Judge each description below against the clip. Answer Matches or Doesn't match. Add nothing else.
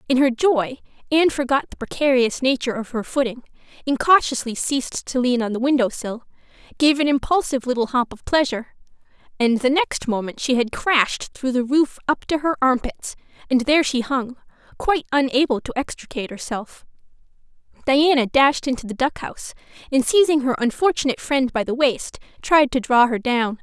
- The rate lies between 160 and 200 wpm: Matches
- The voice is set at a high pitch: Matches